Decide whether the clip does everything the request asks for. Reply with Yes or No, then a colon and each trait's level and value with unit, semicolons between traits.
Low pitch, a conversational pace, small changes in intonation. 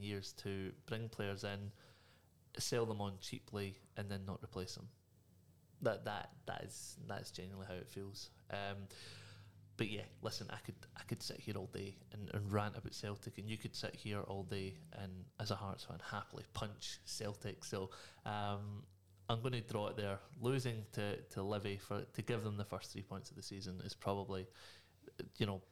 Yes: low, 100 Hz; average, 190 wpm; narrow, 2.3 semitones